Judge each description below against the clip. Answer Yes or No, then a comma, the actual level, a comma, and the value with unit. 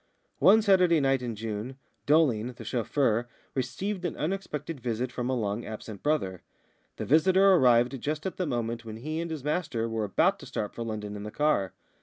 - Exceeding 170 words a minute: Yes, average, 190 wpm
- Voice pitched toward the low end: Yes, low, 125 Hz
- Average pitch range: No, wide, 5.7 semitones